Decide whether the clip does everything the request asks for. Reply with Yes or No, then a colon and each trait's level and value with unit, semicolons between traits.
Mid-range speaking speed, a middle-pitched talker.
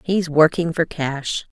Yes: average, 155 wpm; medium, 160 Hz